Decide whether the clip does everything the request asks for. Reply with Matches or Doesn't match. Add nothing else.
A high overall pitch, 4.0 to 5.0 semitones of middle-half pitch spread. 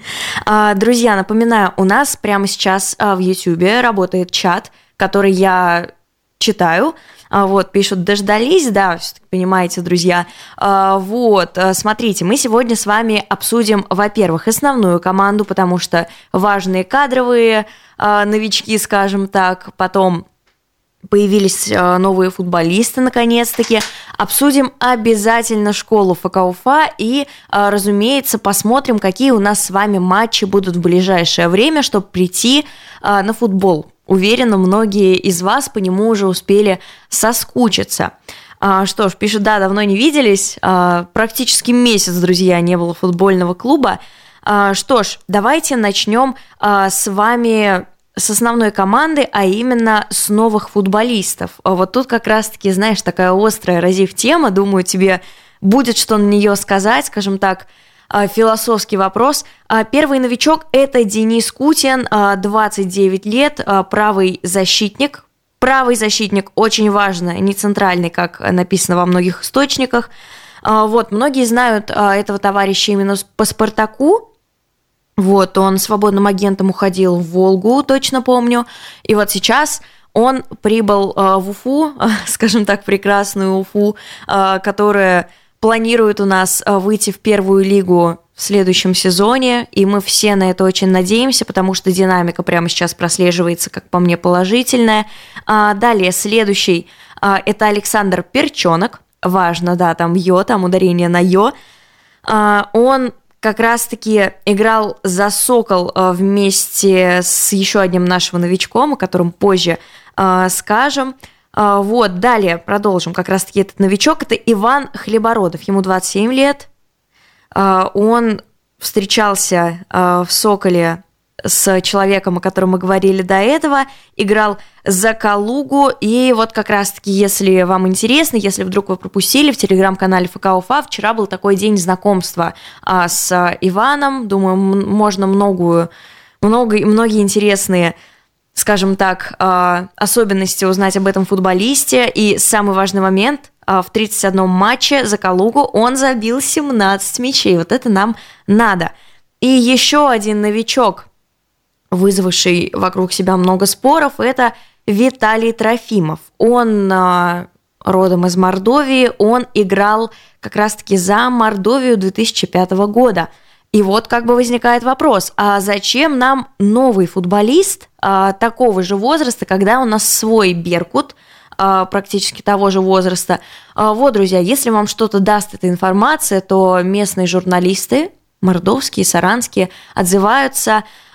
Doesn't match